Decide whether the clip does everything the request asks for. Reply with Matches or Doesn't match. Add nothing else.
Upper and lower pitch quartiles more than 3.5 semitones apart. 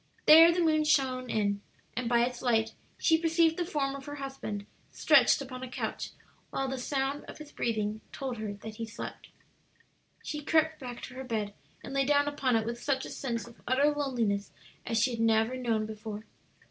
Matches